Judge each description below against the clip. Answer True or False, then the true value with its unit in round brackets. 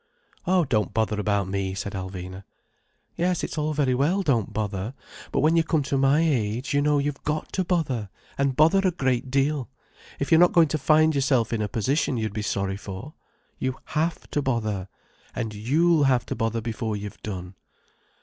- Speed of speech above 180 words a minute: True (190 wpm)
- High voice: False (130 Hz)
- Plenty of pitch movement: True (6.3 semitones)